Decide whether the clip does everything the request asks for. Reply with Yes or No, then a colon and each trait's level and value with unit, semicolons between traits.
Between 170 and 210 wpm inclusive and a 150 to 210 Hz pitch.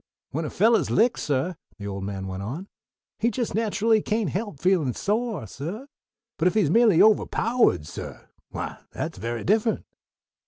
No: average, 160 wpm; high, 190 Hz